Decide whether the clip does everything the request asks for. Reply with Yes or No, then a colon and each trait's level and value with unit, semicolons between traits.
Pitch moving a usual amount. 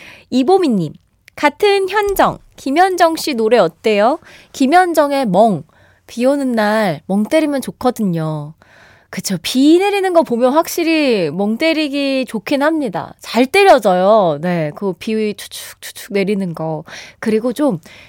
No: wide, 7.7 semitones